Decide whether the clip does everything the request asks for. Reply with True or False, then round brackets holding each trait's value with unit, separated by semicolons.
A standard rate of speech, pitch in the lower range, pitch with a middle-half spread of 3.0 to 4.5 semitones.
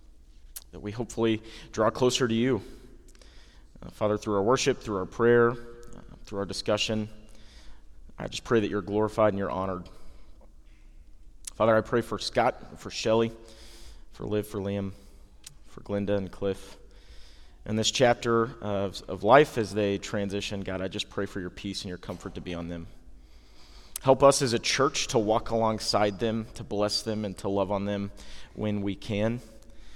False (170 wpm; 105 Hz; 2.6 semitones)